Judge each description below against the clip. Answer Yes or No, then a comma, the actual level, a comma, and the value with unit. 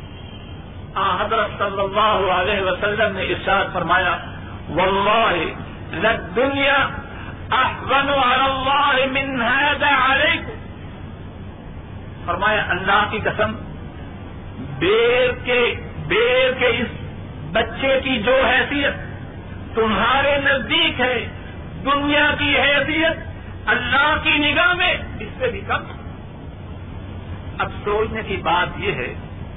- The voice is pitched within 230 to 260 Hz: Yes, very high, 250 Hz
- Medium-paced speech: No, slow, 85 wpm